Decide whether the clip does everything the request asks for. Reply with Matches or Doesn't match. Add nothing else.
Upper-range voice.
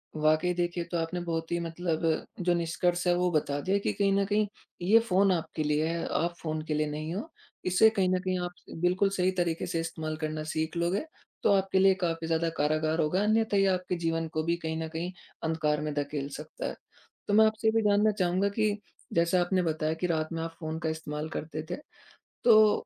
Doesn't match